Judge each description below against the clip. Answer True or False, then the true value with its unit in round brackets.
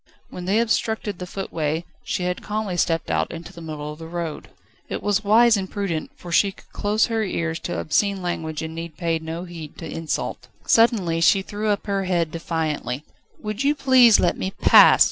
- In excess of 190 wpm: True (200 wpm)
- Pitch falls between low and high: True (180 Hz)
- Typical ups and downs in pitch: True (4.1 semitones)